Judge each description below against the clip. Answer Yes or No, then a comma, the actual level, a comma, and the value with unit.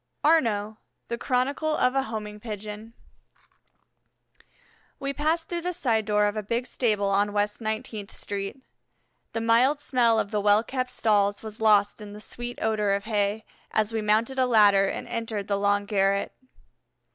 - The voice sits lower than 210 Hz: No, high, 215 Hz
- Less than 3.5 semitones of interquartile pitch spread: Yes, average, 2.9 semitones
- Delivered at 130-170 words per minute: Yes, average, 165 wpm